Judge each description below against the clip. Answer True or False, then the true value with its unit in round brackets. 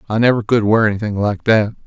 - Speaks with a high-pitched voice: False (110 Hz)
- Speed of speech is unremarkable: False (225 wpm)